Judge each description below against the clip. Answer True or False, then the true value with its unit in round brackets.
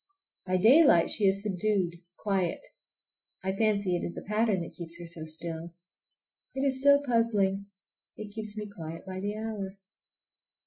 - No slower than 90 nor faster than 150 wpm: False (160 wpm)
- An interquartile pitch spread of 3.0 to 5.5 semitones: True (3.7 semitones)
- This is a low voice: False (195 Hz)